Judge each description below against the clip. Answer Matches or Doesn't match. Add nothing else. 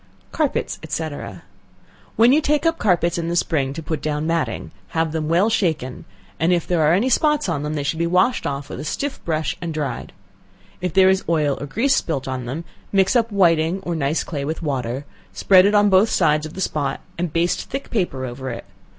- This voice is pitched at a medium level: Matches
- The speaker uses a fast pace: Matches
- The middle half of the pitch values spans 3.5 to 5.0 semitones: Matches